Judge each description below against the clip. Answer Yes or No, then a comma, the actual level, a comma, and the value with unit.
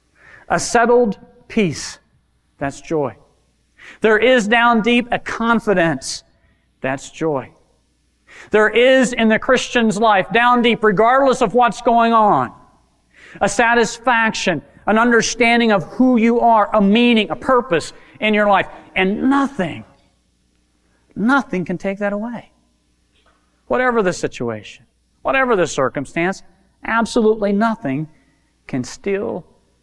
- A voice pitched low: No, high, 210 Hz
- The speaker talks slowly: Yes, slow, 115 wpm